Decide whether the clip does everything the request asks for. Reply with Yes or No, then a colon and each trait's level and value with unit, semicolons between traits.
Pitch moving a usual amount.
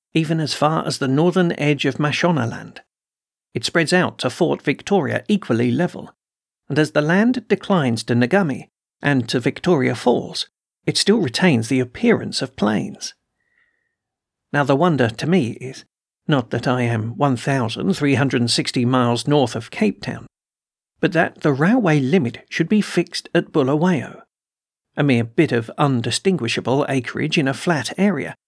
No: wide, 5.9 semitones